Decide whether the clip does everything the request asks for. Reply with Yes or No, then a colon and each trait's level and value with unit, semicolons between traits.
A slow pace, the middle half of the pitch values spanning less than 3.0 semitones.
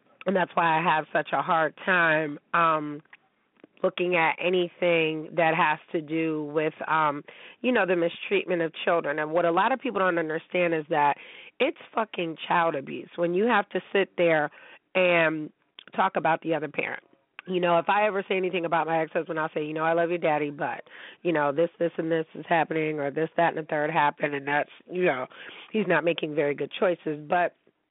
No: fast, 205 wpm; narrow, 2.5 semitones